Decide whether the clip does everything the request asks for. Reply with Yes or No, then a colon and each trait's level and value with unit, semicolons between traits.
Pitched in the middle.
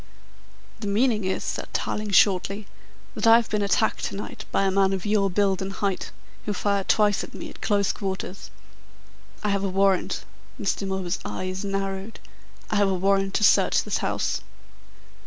No: high, 195 Hz